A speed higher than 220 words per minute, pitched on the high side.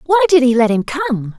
Yes: fast, 260 wpm; very high, 270 Hz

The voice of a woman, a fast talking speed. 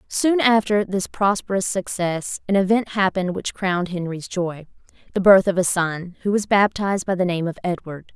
No: female; average, 175 wpm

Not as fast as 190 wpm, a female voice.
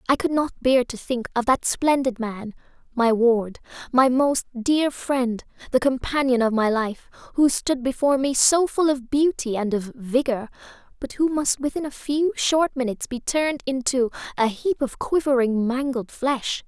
Yes: average, 175 wpm; female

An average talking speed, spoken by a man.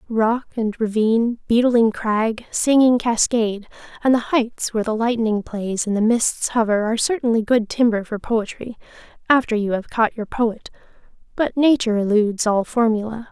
No: average, 150 wpm; female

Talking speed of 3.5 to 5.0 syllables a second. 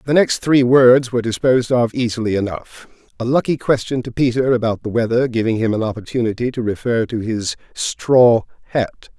No: 5.3 syllables/s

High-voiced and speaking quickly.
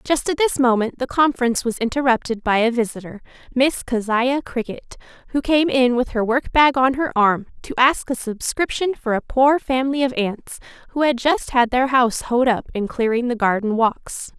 No: very high, 250 Hz; average, 195 wpm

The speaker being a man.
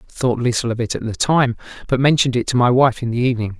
Yes: male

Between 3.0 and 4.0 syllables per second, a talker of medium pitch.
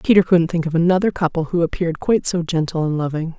No: 6.7 syllables/s; medium, 170 Hz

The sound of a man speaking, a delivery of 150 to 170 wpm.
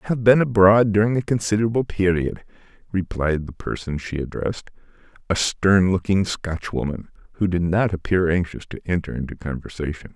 Yes: male; average, 155 wpm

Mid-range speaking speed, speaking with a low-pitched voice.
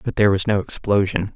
No: fast, 220 wpm; low, 100 Hz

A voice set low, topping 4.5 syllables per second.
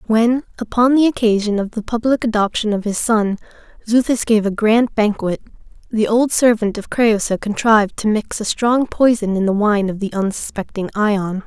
No: high, 220 Hz; 4.9 syllables/s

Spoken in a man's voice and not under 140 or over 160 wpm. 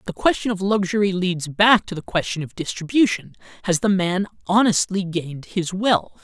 No: male; average, 175 wpm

